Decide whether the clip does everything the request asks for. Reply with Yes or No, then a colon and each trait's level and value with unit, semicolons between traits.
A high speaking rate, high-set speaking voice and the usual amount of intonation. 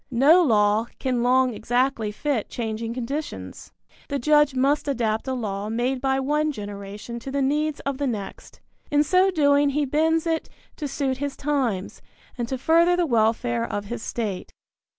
No: average, 170 wpm; very high, 260 Hz; average, 4.2 semitones